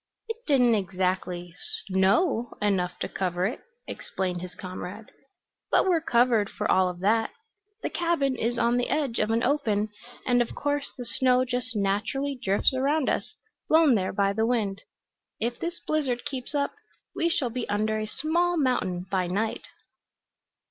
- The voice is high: Yes, high, 230 Hz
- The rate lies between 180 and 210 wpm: No, average, 160 wpm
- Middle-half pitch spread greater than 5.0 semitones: Yes, wide, 5.6 semitones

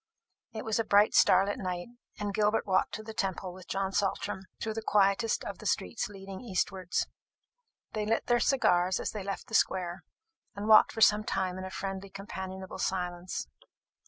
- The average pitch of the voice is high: Yes, high, 195 Hz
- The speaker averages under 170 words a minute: No, average, 185 wpm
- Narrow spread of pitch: Yes, narrow, 2.2 semitones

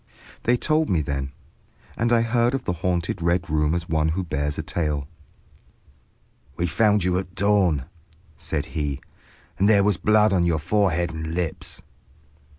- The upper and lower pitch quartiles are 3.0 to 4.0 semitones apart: No, average, 4.7 semitones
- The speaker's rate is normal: Yes, average, 160 wpm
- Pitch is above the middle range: No, very low, 85 Hz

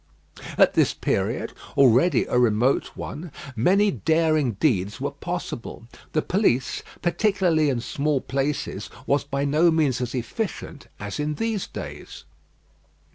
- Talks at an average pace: No, slow, 130 wpm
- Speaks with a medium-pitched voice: Yes, medium, 145 Hz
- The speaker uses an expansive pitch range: No, average, 5.0 semitones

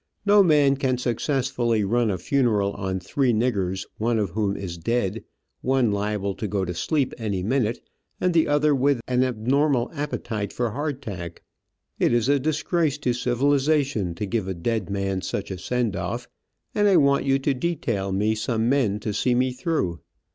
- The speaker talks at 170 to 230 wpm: Yes, average, 175 wpm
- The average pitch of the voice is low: Yes, low, 120 Hz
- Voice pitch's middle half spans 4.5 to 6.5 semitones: Yes, wide, 5.4 semitones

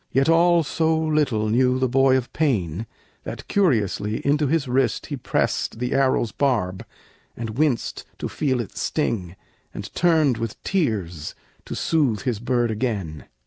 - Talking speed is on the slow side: No, average, 150 wpm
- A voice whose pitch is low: Yes, low, 125 Hz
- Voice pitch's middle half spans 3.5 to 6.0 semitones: Yes, wide, 5.5 semitones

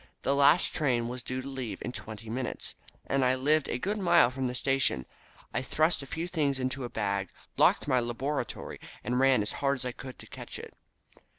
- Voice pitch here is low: Yes, low, 130 Hz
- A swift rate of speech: Yes, fast, 210 wpm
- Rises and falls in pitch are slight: Yes, narrow, 2.3 semitones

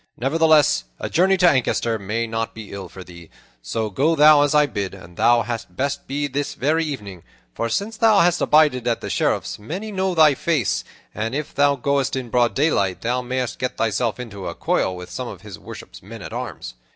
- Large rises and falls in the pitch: Yes, wide, 5.7 semitones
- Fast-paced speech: Yes, fast, 210 wpm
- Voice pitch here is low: Yes, low, 125 Hz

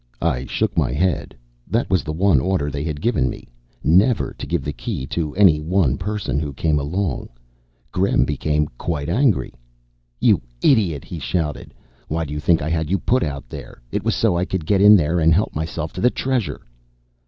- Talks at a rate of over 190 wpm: Yes, average, 200 wpm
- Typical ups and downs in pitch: Yes, average, 4.5 semitones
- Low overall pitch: Yes, very low, 80 Hz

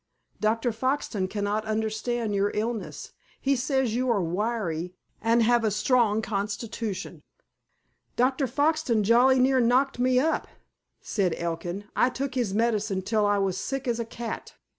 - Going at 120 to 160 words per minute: Yes, average, 145 wpm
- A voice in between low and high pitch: No, high, 225 Hz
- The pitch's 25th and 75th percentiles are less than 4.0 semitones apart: Yes, average, 3.5 semitones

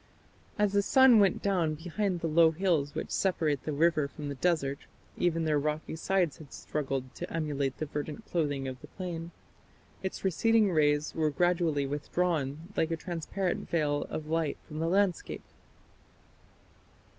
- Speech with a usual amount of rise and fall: Yes, average, 3.4 semitones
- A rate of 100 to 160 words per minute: Yes, average, 155 wpm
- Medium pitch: Yes, medium, 160 Hz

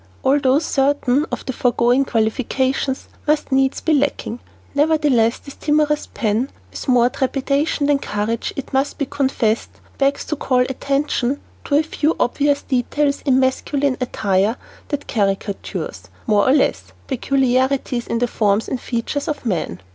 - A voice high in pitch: Yes, very high, 265 Hz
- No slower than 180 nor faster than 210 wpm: No, average, 145 wpm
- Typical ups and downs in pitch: Yes, average, 3.1 semitones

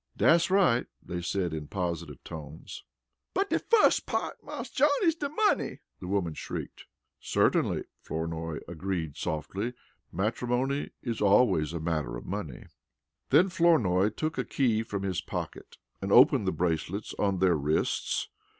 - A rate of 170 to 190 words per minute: No, average, 145 wpm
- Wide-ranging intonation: Yes, wide, 7.4 semitones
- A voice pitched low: Yes, very low, 95 Hz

